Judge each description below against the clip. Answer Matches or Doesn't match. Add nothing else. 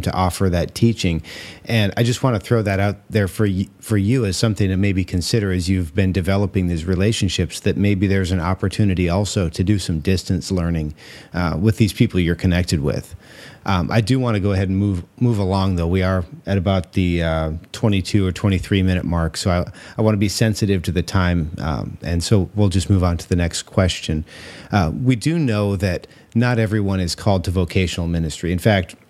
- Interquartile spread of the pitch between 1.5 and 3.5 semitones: Matches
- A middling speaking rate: Doesn't match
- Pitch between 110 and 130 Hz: Doesn't match